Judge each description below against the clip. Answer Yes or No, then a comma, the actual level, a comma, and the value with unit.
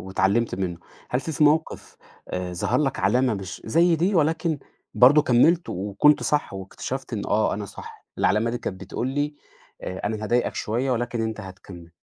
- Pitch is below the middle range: Yes, low, 115 Hz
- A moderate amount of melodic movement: No, wide, 7.0 semitones